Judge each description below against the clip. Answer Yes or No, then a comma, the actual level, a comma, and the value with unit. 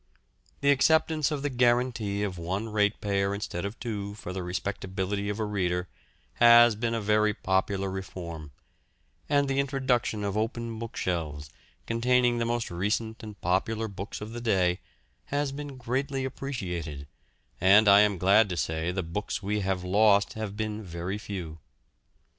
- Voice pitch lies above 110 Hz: No, low, 105 Hz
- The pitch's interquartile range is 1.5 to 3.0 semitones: No, average, 3.8 semitones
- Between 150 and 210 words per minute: Yes, average, 155 wpm